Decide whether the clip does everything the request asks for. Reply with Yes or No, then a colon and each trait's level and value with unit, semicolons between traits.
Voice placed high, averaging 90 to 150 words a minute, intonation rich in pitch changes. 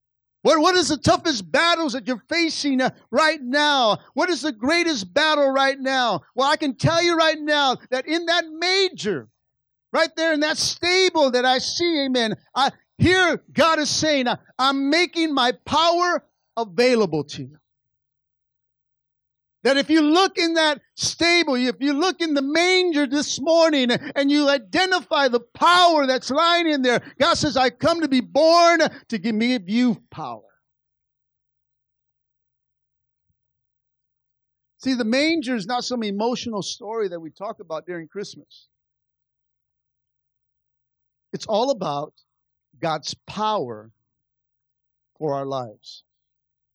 Yes: very high, 275 Hz; average, 140 wpm; wide, 5.8 semitones